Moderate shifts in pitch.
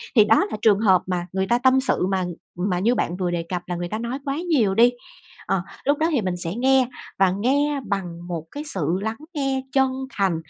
No: wide, 6.3 semitones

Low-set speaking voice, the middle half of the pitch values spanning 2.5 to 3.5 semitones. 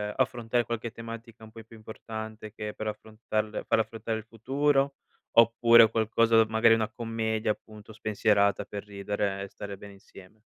No: low, 110 Hz; narrow, 1.4 semitones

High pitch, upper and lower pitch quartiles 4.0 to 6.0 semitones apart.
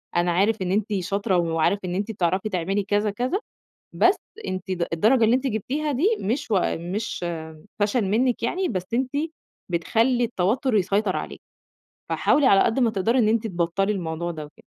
Yes: high, 205 Hz; average, 4.5 semitones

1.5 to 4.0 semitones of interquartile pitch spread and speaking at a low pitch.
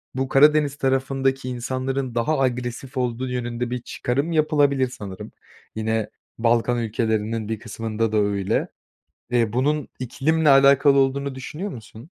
Yes: average, 3.2 semitones; low, 130 Hz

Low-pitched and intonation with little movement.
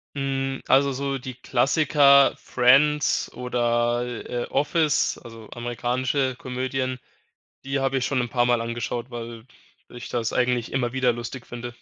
Yes: low, 125 Hz; narrow, 2.0 semitones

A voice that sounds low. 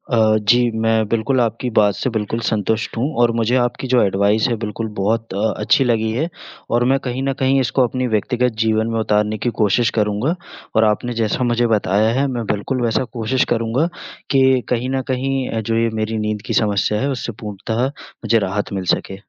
Yes: low, 115 Hz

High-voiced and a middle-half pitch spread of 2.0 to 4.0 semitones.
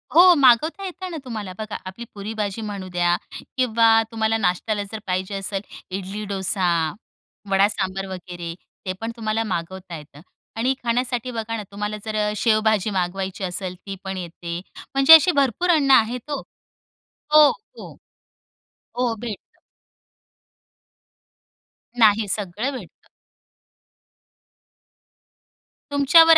No: high, 215 Hz; average, 4.4 semitones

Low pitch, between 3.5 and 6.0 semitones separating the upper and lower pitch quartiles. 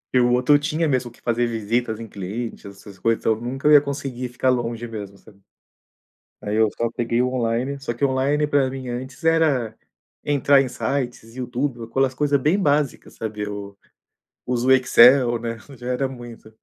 No: low, 125 Hz; average, 2.9 semitones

